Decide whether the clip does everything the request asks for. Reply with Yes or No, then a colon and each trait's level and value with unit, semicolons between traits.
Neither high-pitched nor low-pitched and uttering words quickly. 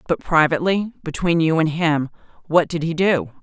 No: medium, 160 Hz; average, 140 wpm